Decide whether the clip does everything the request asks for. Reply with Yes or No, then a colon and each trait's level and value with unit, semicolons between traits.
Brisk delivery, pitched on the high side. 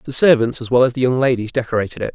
No: fast, 280 wpm; low, 125 Hz